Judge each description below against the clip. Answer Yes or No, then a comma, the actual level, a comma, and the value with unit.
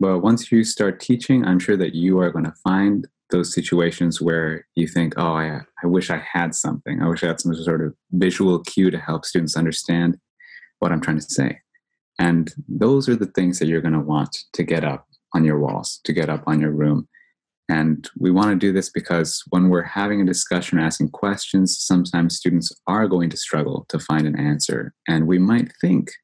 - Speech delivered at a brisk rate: Yes, fast, 215 wpm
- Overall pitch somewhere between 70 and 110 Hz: Yes, very low, 85 Hz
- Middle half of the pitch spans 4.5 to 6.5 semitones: No, average, 2.8 semitones